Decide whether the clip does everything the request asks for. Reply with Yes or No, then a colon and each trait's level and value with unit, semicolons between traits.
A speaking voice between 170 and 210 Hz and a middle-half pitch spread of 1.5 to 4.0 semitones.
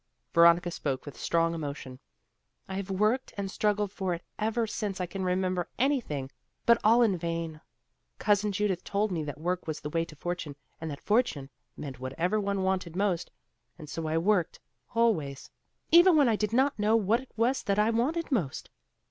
No: high, 190 Hz; average, 4.6 semitones